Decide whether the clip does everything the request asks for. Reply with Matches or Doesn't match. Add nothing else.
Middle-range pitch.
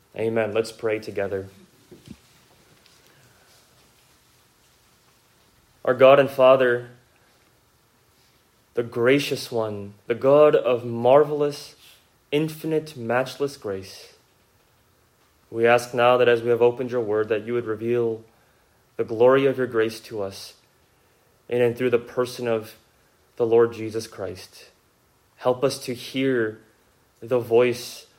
Doesn't match